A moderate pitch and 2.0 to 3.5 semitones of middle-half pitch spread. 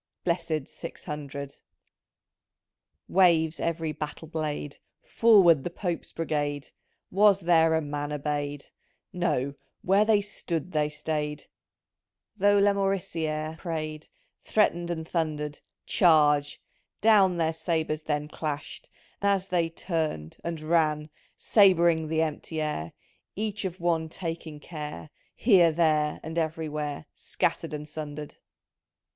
Yes: medium, 160 Hz; narrow, 2.5 semitones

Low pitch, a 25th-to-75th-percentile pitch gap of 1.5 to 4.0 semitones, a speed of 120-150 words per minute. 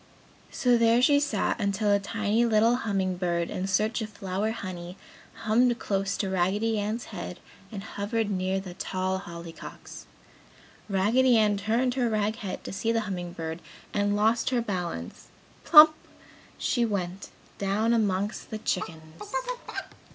No: high, 205 Hz; average, 3.2 semitones; average, 145 wpm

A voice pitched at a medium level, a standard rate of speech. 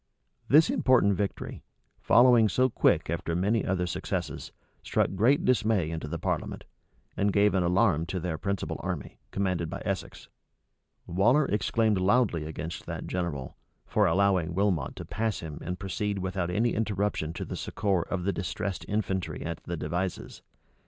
No: very low, 95 Hz; average, 155 wpm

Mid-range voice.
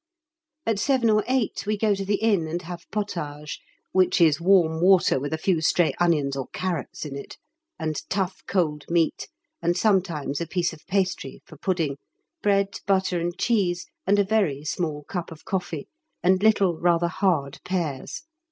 Yes: medium, 175 Hz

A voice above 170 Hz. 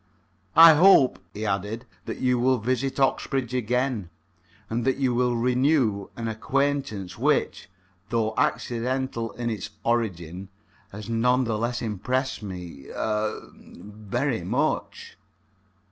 No: low, 120 Hz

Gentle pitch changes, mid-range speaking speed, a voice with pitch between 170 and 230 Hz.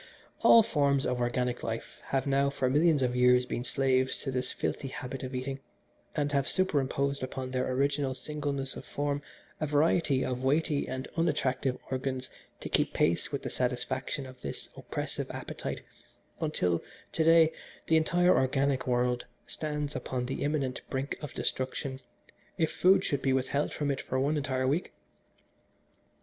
No: narrow, 2.1 semitones; average, 160 wpm; low, 135 Hz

